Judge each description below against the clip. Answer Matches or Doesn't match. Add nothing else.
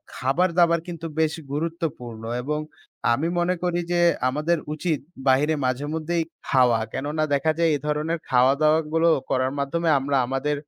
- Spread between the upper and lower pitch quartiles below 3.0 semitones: Doesn't match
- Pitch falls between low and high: Matches